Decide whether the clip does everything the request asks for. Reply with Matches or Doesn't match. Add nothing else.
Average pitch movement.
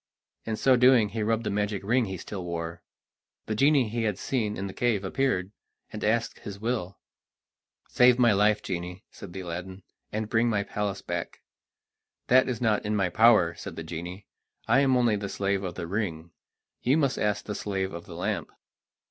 Matches